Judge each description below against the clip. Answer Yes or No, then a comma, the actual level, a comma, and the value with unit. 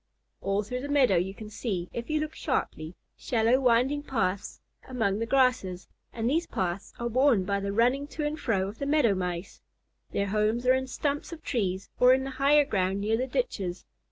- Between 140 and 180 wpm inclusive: No, average, 200 wpm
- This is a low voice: No, high, 235 Hz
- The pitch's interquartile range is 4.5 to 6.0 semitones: Yes, average, 5.3 semitones